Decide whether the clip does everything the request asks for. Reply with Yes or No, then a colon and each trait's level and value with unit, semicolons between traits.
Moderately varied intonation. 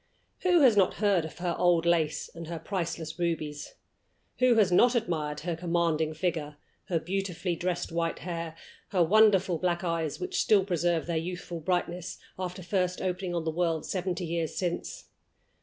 No: narrow, 2.1 semitones